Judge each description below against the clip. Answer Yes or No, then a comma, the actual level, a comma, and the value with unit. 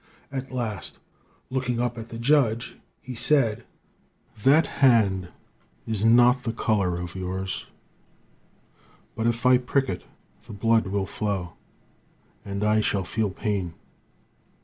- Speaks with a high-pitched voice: No, low, 115 Hz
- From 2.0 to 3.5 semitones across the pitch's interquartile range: No, average, 3.9 semitones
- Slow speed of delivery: Yes, slow, 125 wpm